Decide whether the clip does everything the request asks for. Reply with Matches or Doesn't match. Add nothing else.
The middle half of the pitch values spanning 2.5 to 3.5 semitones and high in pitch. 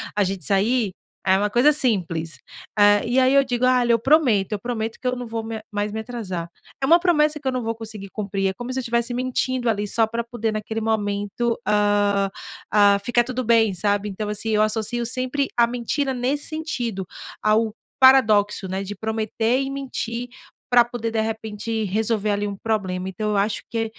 Matches